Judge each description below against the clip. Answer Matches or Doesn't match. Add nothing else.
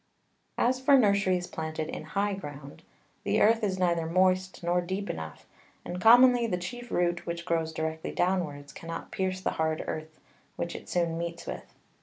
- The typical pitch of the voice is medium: Matches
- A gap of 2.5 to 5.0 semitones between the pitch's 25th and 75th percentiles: Matches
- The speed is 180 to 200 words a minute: Doesn't match